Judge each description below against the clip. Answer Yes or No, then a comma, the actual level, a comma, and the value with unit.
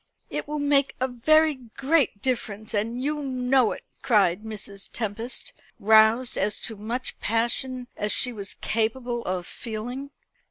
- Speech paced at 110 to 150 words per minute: Yes, average, 145 wpm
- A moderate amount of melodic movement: Yes, average, 3.4 semitones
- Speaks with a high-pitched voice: Yes, high, 235 Hz